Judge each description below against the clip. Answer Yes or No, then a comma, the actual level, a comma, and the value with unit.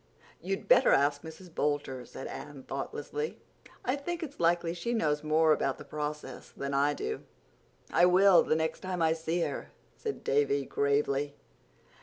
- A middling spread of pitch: Yes, average, 4.0 semitones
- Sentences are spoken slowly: No, average, 160 wpm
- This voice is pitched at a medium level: Yes, medium, 160 Hz